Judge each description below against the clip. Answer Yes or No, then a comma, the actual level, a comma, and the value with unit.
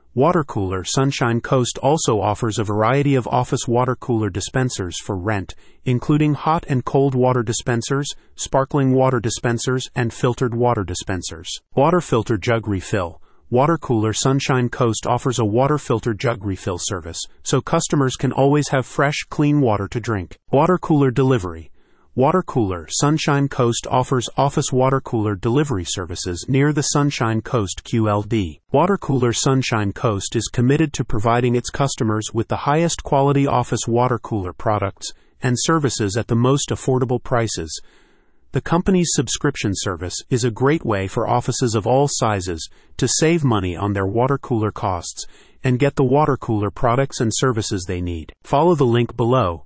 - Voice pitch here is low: Yes, low, 125 Hz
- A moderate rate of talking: Yes, average, 160 wpm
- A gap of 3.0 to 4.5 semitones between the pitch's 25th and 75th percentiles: Yes, average, 4.2 semitones